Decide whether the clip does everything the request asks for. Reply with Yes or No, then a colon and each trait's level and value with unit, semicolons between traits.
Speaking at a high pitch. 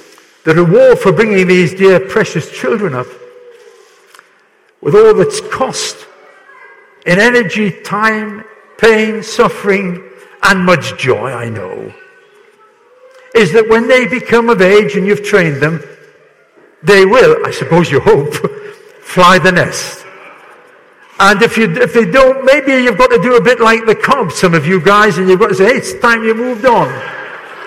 Yes: high, 235 Hz